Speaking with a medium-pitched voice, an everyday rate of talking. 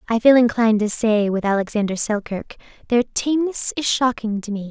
No: high, 225 Hz; average, 180 wpm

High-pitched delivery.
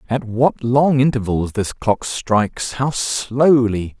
No: low, 120 Hz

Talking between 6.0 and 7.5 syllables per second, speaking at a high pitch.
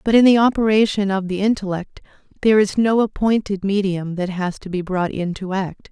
No: 5.4 syllables/s; high, 200 Hz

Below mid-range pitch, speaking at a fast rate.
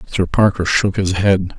No: very low, 95 Hz; average, 190 wpm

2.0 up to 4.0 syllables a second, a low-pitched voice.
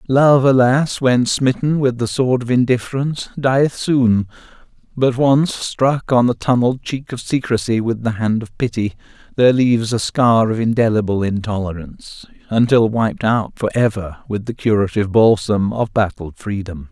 No: 4.7 syllables/s; low, 115 Hz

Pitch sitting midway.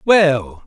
Yes: medium, 165 Hz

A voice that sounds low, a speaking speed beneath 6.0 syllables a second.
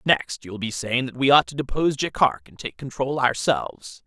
Yes: low, 120 Hz; 5.1 syllables/s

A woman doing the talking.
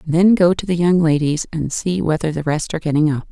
Yes: female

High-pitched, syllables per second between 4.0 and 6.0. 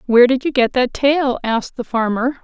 Yes: very high, 250 Hz; 5.3 syllables/s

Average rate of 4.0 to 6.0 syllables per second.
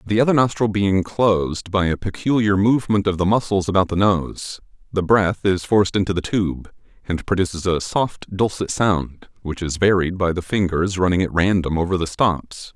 Yes: 5.0 syllables/s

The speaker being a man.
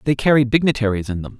Yes: male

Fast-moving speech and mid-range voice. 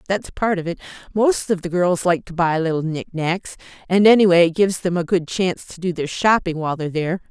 Yes: fast, 240 wpm; medium, 175 Hz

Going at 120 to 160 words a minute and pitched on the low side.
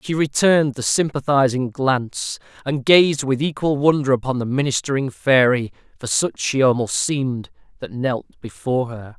Yes: average, 150 wpm; low, 130 Hz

